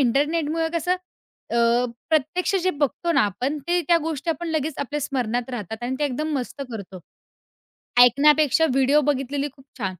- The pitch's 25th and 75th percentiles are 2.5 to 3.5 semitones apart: No, average, 4.0 semitones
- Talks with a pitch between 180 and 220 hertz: No, very high, 285 Hz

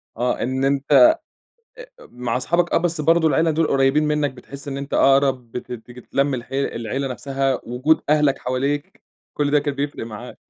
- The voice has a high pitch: No, medium, 140 Hz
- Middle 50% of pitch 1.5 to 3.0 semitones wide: Yes, average, 2.7 semitones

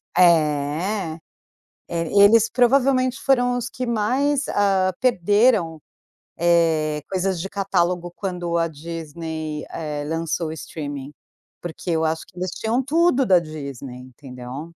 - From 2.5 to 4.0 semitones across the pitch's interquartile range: No, average, 5.2 semitones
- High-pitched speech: No, medium, 170 Hz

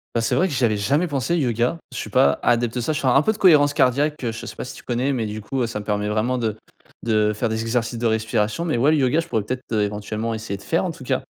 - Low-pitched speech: Yes, low, 120 Hz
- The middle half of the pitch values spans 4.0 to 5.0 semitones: Yes, average, 4.3 semitones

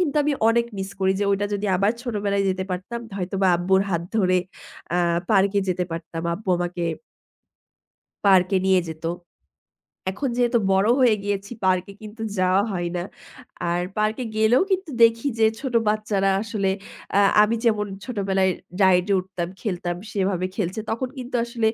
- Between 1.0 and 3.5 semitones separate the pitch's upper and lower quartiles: Yes, average, 3.1 semitones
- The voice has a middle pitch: No, high, 200 Hz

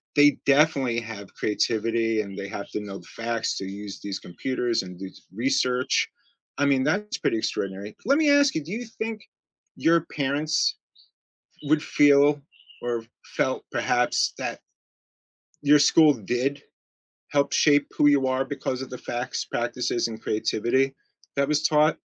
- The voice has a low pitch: Yes, low, 130 Hz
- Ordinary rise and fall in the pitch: Yes, average, 4.6 semitones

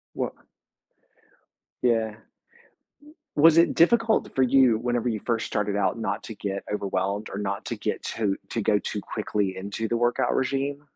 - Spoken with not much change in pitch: No, average, 3.7 semitones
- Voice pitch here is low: Yes, low, 110 Hz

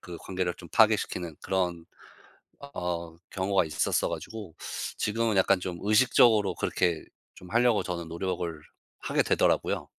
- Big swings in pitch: No, average, 3.4 semitones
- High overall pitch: No, very low, 95 Hz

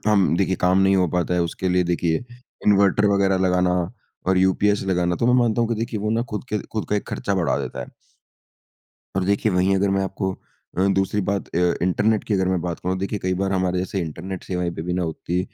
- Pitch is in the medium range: No, very low, 95 Hz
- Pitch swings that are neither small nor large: No, narrow, 2.0 semitones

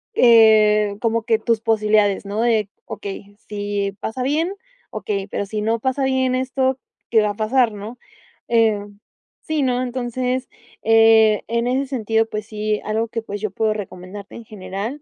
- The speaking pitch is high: Yes, high, 220 Hz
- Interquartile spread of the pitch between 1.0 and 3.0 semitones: Yes, average, 2.7 semitones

